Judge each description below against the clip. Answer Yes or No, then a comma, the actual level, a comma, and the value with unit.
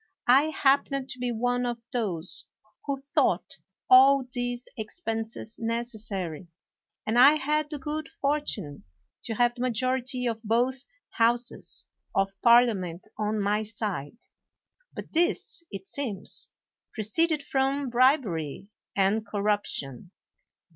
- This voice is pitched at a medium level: No, high, 240 Hz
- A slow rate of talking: Yes, slow, 115 wpm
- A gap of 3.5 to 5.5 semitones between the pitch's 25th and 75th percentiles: Yes, average, 4.1 semitones